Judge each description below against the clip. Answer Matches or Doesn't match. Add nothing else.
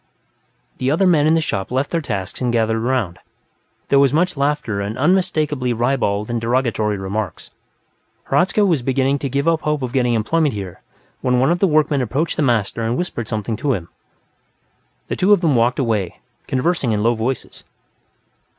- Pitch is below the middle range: Matches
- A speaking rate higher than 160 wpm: Matches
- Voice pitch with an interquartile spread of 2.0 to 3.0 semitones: Doesn't match